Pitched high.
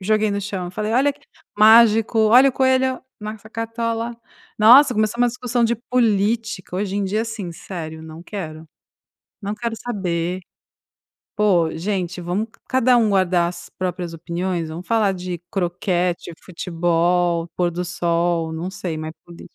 Yes: high, 195 Hz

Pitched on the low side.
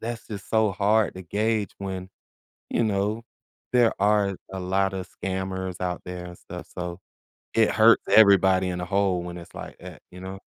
Yes: very low, 95 Hz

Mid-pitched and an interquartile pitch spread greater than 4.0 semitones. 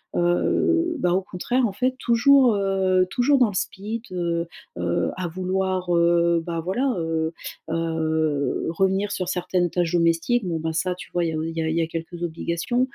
No: medium, 180 Hz; average, 3.2 semitones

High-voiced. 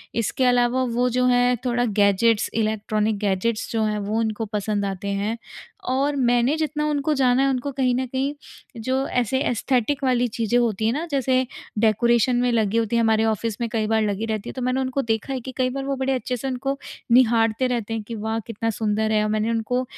Yes: high, 235 Hz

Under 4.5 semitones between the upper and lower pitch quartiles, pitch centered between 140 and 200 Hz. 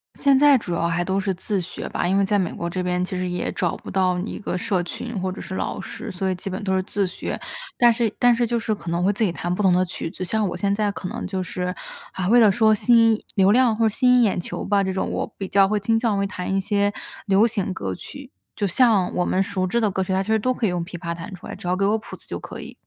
Yes: average, 3.2 semitones; high, 195 Hz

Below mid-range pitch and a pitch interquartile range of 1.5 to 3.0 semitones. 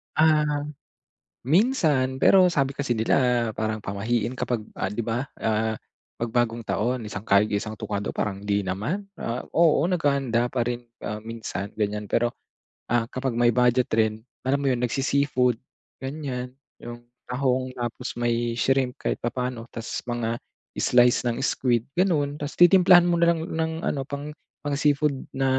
No: low, 125 Hz; average, 3.6 semitones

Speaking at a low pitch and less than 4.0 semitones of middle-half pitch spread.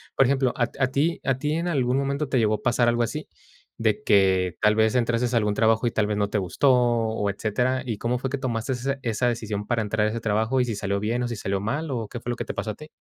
Yes: low, 120 Hz; average, 3.2 semitones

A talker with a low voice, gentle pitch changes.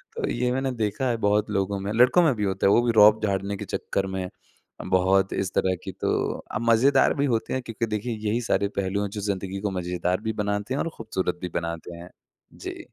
No: low, 100 Hz; average, 3.4 semitones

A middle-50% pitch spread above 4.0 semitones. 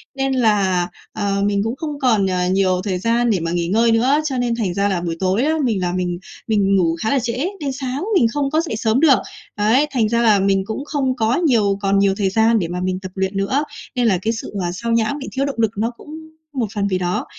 Yes: average, 4.9 semitones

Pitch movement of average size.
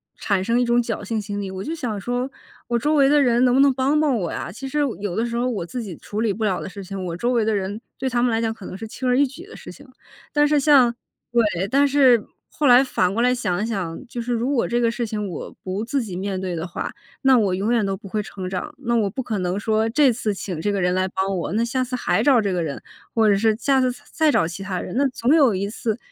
Yes: average, 4.5 semitones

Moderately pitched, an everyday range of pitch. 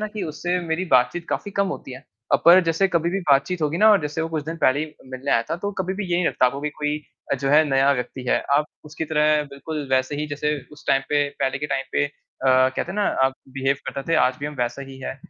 Yes: medium, 150 Hz; average, 3.4 semitones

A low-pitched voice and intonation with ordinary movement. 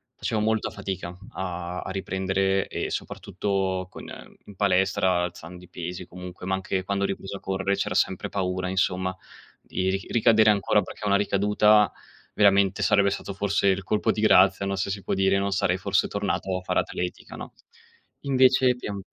No: very low, 95 Hz; narrow, 1.4 semitones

